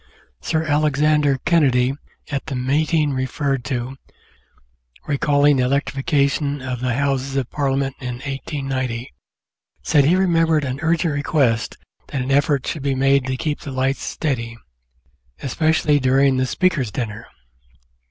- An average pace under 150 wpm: Yes, slow, 135 wpm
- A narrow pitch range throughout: Yes, narrow, 2.3 semitones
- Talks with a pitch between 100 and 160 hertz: Yes, medium, 140 Hz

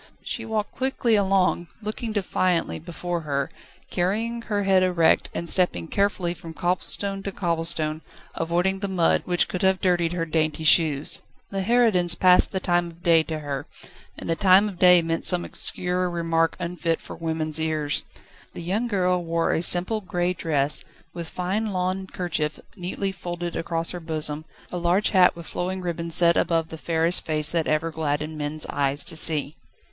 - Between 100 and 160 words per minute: No, average, 170 wpm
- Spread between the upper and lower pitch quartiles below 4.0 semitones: Yes, narrow, 2.5 semitones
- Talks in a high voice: No, medium, 175 Hz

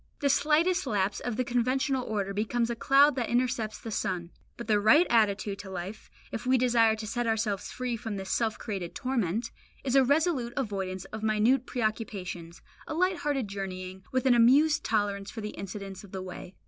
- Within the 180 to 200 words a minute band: Yes, average, 190 wpm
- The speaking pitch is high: Yes, high, 225 Hz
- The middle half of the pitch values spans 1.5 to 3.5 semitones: No, average, 4.3 semitones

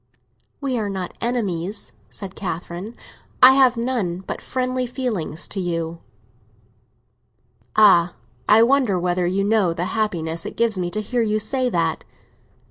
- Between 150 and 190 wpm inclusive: No, average, 140 wpm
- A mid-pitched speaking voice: No, high, 205 Hz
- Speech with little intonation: No, average, 5.2 semitones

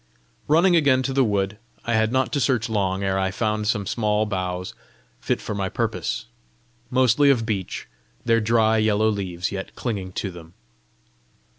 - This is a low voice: Yes, low, 110 Hz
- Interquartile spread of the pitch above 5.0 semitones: No, average, 3.6 semitones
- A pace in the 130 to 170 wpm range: Yes, average, 165 wpm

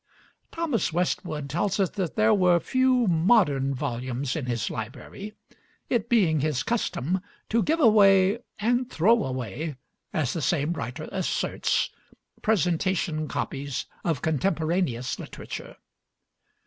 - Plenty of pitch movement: Yes, wide, 6.8 semitones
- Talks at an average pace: No, slow, 120 wpm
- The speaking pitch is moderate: Yes, medium, 170 Hz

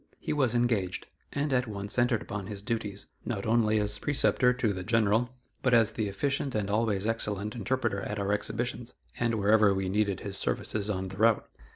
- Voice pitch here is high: No, low, 110 Hz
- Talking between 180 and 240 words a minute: Yes, average, 190 wpm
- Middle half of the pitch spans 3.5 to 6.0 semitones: No, average, 2.9 semitones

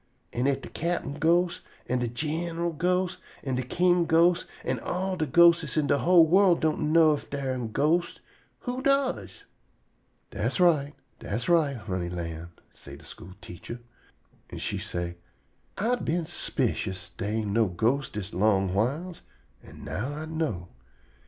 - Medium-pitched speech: Yes, medium, 145 Hz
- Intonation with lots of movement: Yes, wide, 7.7 semitones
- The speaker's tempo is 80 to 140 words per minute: No, average, 160 wpm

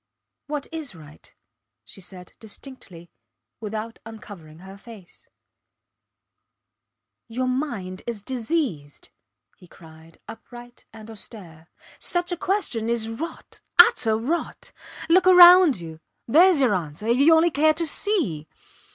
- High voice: Yes, high, 225 Hz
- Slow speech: Yes, slow, 120 wpm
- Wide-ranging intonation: Yes, wide, 8.8 semitones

